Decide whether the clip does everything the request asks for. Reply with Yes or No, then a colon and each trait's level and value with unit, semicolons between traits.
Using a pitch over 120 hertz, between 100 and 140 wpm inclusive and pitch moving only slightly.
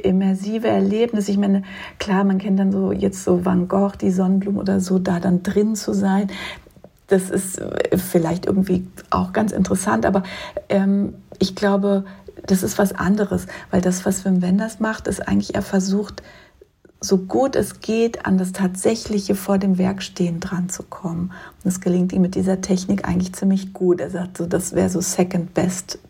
No: high, 190 Hz; average, 175 wpm; narrow, 1.4 semitones